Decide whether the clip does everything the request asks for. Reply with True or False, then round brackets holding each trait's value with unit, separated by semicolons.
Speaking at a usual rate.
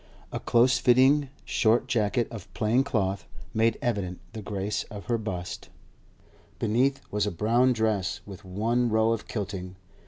True (150 wpm)